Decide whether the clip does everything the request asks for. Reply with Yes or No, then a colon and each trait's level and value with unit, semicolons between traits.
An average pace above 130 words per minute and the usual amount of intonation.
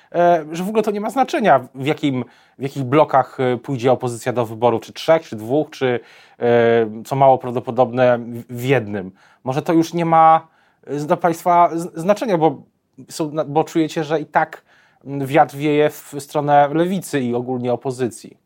Yes: average, 155 wpm; average, 4.5 semitones